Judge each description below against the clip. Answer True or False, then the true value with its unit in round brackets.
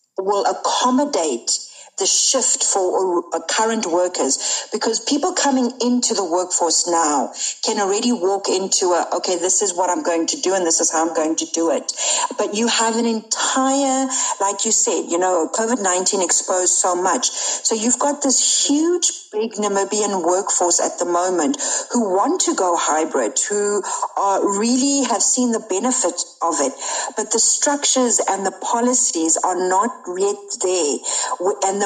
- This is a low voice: False (210 Hz)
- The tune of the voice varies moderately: False (5.9 semitones)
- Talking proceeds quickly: False (165 wpm)